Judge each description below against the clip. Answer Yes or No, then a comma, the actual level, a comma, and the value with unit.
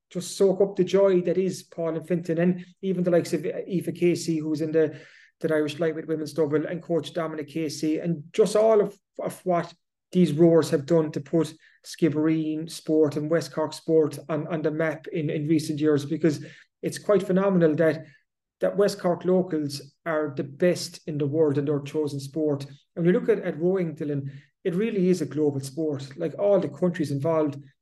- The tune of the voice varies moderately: No, narrow, 2.3 semitones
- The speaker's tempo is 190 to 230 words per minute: Yes, average, 200 wpm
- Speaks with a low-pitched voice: No, medium, 160 Hz